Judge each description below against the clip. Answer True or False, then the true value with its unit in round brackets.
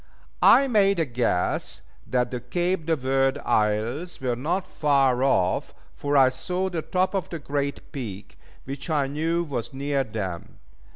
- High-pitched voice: False (140 Hz)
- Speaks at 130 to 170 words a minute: True (160 wpm)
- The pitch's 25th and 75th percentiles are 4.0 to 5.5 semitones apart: True (5.2 semitones)